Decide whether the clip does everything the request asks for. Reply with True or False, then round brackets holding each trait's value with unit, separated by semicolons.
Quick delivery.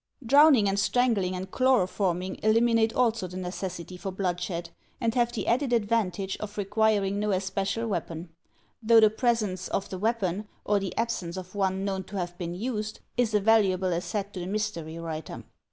False (170 wpm)